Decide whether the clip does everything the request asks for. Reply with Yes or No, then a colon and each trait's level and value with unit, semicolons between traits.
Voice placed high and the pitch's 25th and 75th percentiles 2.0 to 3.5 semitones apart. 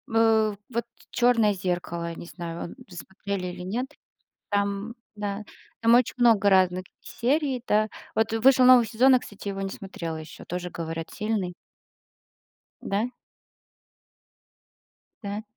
No: high, 205 Hz; average, 4.1 semitones